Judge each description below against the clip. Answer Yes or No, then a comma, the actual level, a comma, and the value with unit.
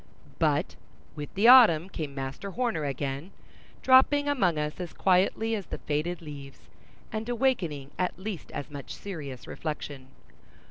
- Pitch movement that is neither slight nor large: No, wide, 7.0 semitones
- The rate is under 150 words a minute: Yes, average, 140 wpm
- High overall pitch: No, medium, 170 Hz